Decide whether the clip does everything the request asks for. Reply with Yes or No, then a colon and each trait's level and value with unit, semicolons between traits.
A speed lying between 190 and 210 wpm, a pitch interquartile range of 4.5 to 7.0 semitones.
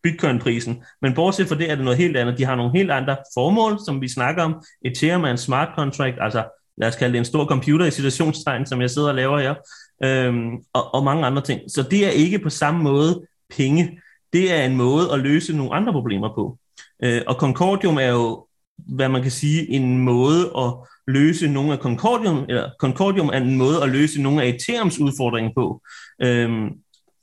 No: average, 205 wpm; average, 4.1 semitones